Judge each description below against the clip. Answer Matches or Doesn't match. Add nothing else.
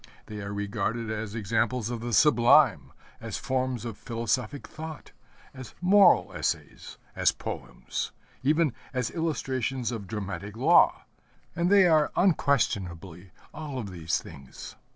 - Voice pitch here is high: Doesn't match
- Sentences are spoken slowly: Matches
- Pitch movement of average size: Doesn't match